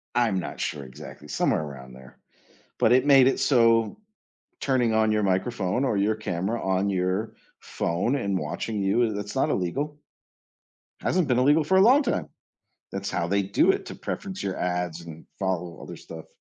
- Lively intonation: Yes, wide, 5.7 semitones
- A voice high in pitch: No, low, 100 Hz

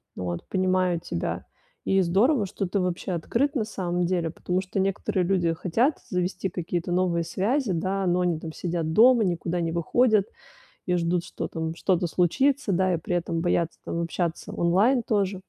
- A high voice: No, medium, 180 Hz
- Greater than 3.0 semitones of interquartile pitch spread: No, narrow, 2.5 semitones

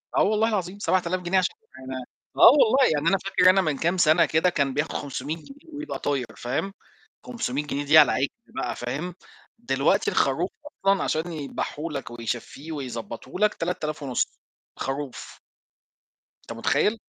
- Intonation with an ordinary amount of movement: No, wide, 5.8 semitones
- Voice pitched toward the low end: No, medium, 160 Hz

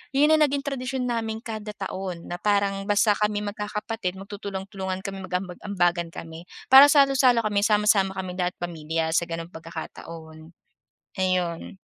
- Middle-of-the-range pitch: No, high, 195 Hz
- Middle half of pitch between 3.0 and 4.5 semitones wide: Yes, average, 3.6 semitones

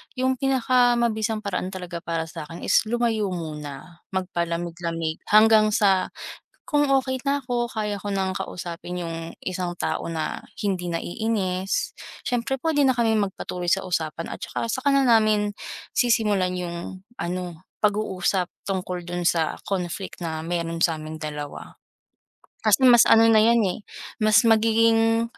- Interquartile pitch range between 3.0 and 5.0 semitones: Yes, average, 4.7 semitones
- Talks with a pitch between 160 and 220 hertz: Yes, high, 190 Hz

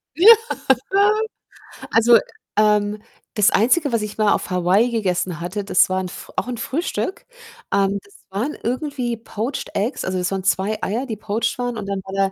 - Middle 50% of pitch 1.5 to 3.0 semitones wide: No, average, 3.6 semitones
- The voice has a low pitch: No, high, 210 Hz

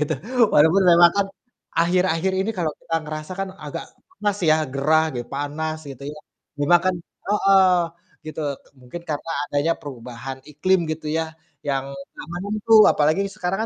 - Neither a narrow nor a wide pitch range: Yes, average, 4.3 semitones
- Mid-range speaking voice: Yes, medium, 160 Hz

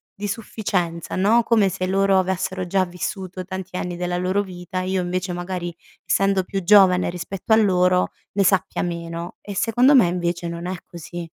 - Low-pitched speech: No, medium, 185 Hz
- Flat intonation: Yes, narrow, 1.8 semitones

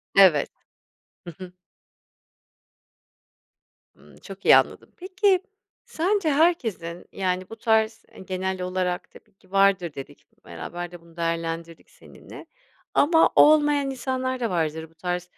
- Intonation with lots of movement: Yes, wide, 7.5 semitones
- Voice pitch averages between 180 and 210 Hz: Yes, high, 190 Hz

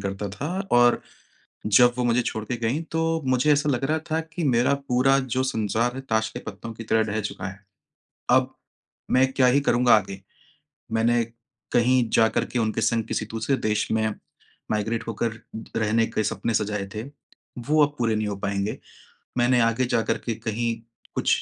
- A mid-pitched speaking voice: No, low, 115 Hz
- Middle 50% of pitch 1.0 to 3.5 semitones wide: Yes, average, 2.8 semitones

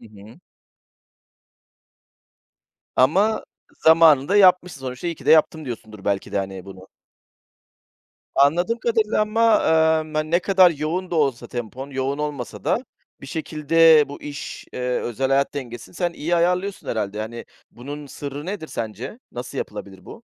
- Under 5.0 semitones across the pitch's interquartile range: No, wide, 5.6 semitones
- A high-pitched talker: No, medium, 150 Hz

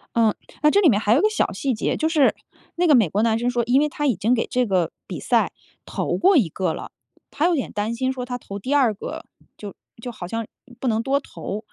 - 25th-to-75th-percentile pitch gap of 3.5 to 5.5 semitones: Yes, average, 4.8 semitones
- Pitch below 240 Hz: No, high, 245 Hz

